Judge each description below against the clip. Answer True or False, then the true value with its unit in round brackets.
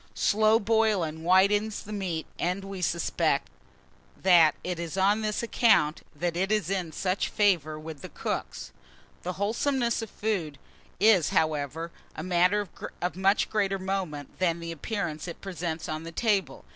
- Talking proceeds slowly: False (155 wpm)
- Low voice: False (185 Hz)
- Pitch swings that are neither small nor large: True (3.9 semitones)